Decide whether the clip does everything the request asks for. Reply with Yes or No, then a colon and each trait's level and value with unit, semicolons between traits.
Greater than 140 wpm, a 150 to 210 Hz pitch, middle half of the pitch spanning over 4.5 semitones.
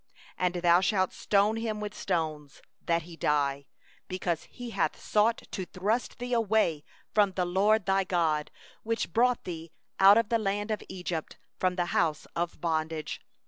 No: average, 170 wpm; medium, 185 Hz; average, 4.1 semitones